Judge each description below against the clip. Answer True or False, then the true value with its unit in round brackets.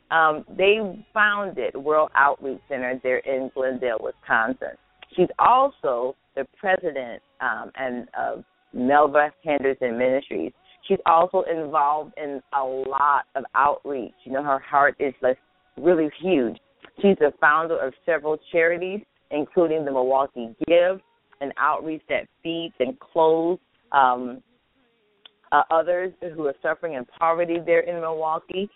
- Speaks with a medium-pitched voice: True (155 Hz)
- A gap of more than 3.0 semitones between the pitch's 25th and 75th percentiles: True (4.5 semitones)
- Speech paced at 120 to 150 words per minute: True (135 wpm)